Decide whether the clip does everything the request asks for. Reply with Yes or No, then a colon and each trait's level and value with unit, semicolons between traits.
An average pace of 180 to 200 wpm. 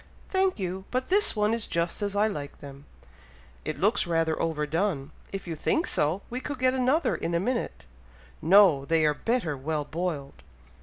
Yes: average, 185 wpm